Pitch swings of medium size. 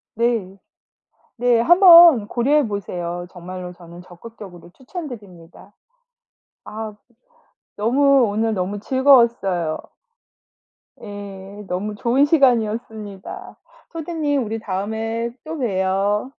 Yes: average, 4.8 semitones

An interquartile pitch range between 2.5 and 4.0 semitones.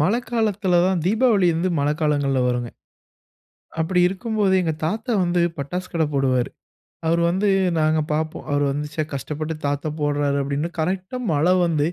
No: average, 4.4 semitones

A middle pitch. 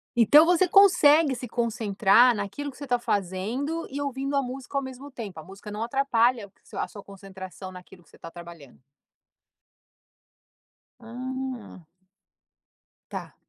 No: high, 240 Hz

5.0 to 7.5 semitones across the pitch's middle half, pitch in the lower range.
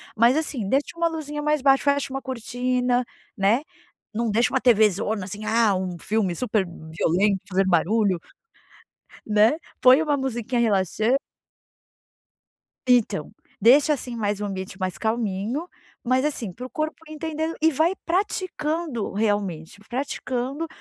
No: wide, 5.6 semitones; high, 235 Hz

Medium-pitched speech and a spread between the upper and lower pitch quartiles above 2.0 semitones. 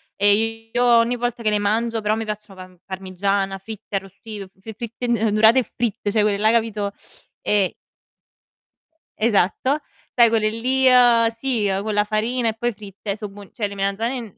No: high, 215 Hz; narrow, 2.4 semitones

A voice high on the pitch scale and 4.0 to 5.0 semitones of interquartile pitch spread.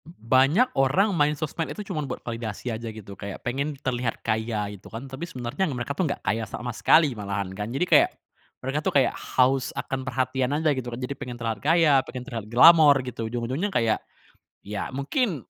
No: low, 130 Hz; average, 4.5 semitones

